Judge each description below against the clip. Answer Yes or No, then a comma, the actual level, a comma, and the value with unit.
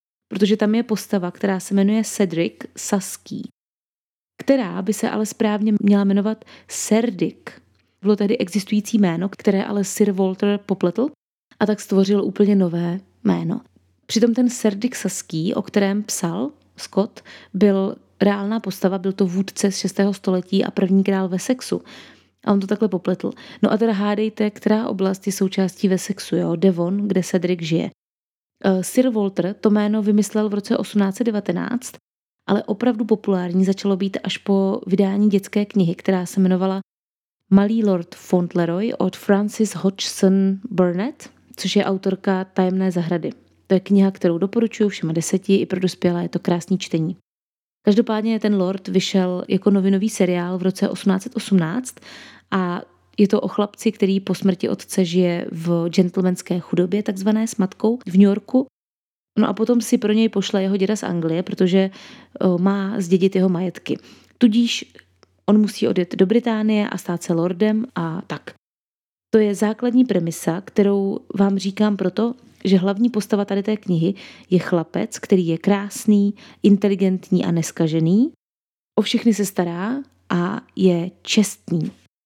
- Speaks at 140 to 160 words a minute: Yes, average, 150 wpm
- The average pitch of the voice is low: No, high, 200 Hz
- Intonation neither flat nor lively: No, narrow, 2.3 semitones